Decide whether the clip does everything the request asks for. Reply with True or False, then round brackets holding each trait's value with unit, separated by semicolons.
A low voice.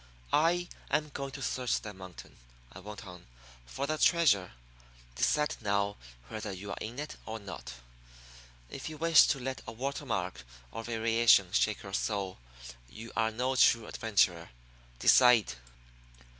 True (110 Hz)